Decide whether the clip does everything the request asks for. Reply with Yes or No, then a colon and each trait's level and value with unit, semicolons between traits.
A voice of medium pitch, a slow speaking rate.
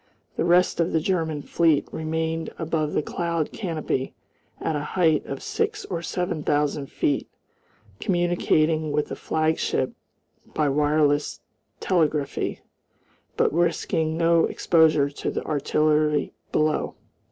Yes: medium, 160 Hz; slow, 120 wpm